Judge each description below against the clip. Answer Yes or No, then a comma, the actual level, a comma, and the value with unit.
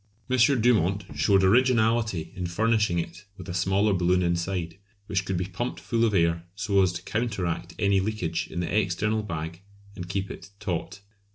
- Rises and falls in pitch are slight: No, average, 3.6 semitones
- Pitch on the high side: No, very low, 95 Hz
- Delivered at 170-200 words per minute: Yes, average, 175 wpm